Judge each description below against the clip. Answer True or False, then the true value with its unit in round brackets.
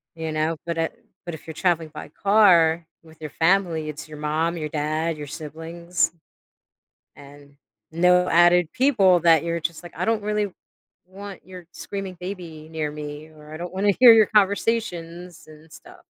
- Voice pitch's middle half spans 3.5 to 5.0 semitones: False (2.8 semitones)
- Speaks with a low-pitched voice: False (170 Hz)